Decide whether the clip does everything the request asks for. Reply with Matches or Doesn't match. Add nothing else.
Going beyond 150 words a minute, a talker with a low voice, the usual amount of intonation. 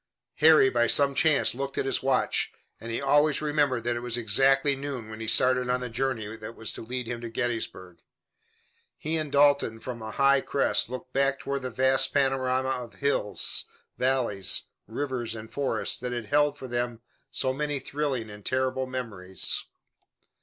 Matches